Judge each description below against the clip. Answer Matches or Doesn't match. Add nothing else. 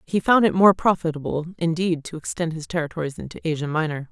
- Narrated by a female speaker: Matches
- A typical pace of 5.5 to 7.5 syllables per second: Matches